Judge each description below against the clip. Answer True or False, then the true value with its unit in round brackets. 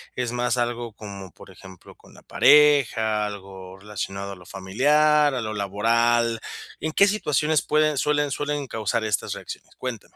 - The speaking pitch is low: True (115 Hz)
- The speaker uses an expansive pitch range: True (6.6 semitones)